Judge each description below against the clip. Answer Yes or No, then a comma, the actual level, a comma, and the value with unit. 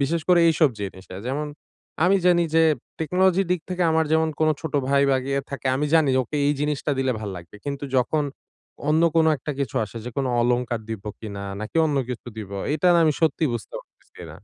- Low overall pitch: No, medium, 145 Hz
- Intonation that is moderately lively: Yes, average, 4.7 semitones